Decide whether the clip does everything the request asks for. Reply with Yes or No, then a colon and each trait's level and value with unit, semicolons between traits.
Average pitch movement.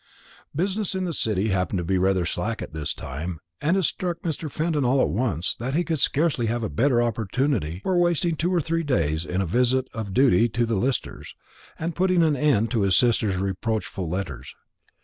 No: wide, 8.7 semitones